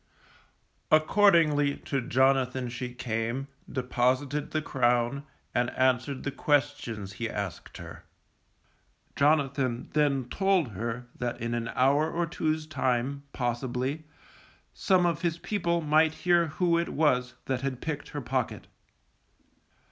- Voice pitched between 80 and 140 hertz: Yes, low, 135 Hz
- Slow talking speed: Yes, slow, 125 wpm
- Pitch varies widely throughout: No, average, 3.9 semitones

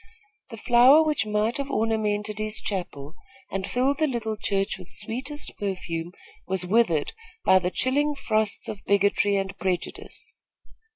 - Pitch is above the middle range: Yes, high, 215 Hz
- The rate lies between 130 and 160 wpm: Yes, average, 140 wpm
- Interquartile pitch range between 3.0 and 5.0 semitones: Yes, average, 4.4 semitones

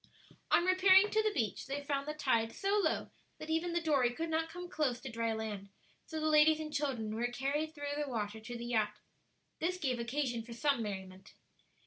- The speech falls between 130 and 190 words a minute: No, fast, 205 wpm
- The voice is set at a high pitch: Yes, very high, 280 Hz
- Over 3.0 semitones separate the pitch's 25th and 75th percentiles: Yes, wide, 5.5 semitones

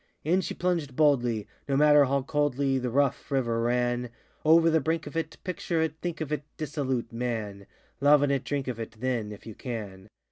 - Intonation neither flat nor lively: Yes, average, 4.0 semitones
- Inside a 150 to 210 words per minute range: Yes, average, 190 wpm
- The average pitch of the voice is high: No, low, 135 Hz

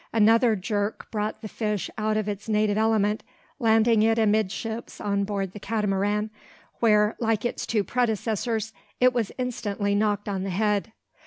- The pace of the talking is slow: No, average, 155 wpm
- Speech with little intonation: Yes, narrow, 1.5 semitones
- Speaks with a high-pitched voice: Yes, high, 215 Hz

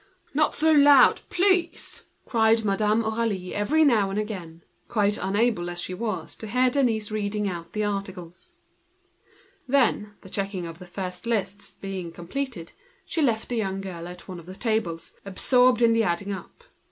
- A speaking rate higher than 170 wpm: No, average, 155 wpm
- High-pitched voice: Yes, high, 210 Hz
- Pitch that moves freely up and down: No, average, 4.1 semitones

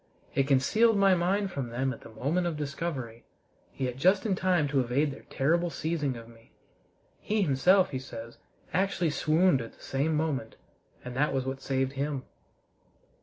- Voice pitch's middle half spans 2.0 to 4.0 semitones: No, average, 4.9 semitones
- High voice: No, medium, 140 Hz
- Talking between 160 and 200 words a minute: Yes, average, 170 wpm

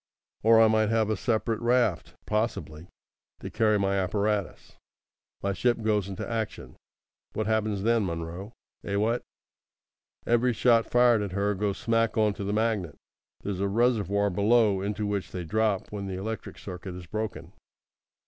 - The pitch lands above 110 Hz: No, low, 105 Hz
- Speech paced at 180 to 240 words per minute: No, average, 160 wpm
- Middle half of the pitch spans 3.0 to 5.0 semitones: No, narrow, 2.4 semitones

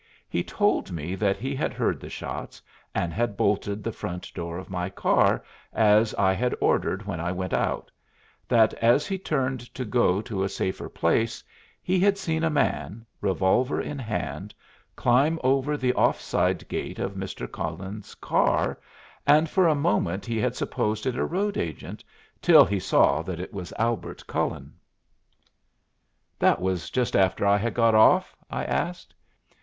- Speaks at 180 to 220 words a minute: No, average, 170 wpm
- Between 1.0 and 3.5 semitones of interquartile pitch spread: No, wide, 5.6 semitones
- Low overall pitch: Yes, low, 110 Hz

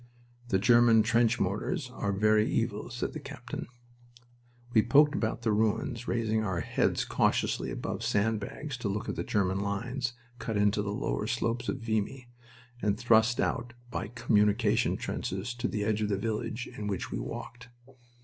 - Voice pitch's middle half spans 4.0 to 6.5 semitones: No, average, 2.7 semitones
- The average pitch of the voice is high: No, low, 110 Hz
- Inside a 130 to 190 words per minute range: Yes, average, 170 wpm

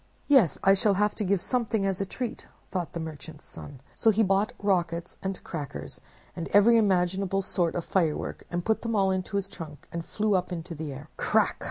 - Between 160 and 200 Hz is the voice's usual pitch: Yes, high, 190 Hz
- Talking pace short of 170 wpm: No, fast, 205 wpm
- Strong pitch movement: No, average, 3.5 semitones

